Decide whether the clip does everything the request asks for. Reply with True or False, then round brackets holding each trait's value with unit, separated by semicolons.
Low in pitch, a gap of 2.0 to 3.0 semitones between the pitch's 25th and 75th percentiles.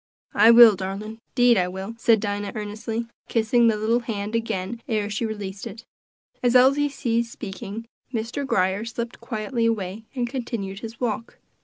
False (225 Hz; 2.5 semitones)